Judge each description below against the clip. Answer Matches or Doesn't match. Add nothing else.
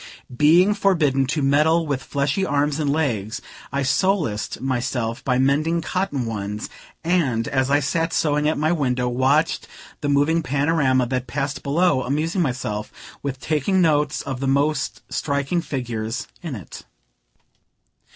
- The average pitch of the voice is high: Doesn't match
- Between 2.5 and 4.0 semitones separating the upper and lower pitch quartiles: Matches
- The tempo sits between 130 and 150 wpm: Matches